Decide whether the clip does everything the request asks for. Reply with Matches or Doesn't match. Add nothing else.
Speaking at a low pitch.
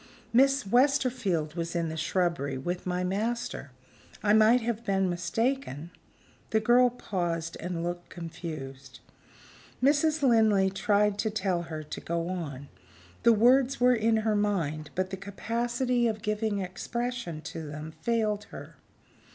Doesn't match